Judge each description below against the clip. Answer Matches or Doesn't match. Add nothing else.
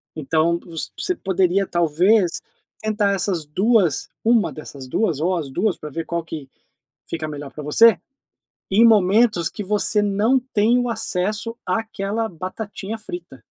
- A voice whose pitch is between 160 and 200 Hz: Matches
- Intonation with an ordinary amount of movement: Matches